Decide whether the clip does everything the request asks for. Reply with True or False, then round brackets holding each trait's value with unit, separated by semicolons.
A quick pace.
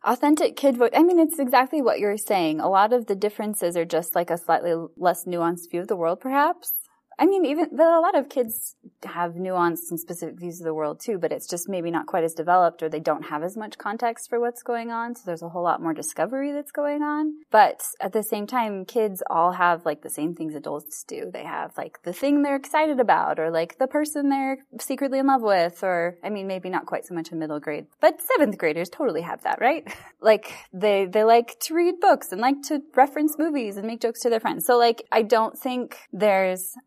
True (235 wpm)